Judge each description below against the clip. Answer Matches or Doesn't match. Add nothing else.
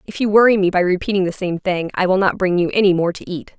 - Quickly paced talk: Matches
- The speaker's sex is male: Doesn't match